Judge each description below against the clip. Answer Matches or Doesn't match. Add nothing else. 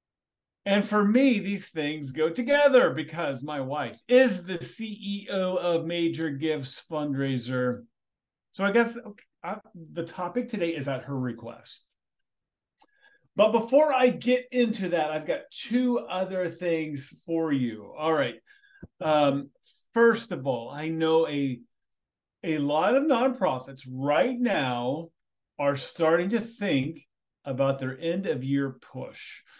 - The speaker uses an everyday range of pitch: Doesn't match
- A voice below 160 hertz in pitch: Doesn't match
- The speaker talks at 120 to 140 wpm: Matches